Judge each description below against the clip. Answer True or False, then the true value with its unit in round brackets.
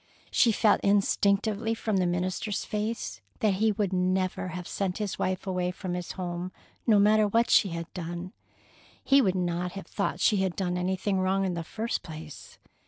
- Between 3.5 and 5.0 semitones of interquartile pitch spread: False (2.6 semitones)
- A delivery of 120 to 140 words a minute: False (180 wpm)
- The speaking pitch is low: False (190 Hz)